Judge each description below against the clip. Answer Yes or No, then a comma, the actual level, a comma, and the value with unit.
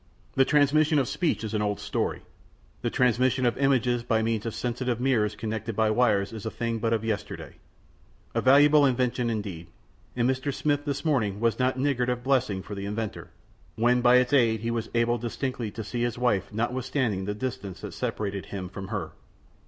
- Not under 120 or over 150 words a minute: No, average, 190 wpm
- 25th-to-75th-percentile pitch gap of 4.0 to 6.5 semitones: No, average, 3.2 semitones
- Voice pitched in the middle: No, low, 120 Hz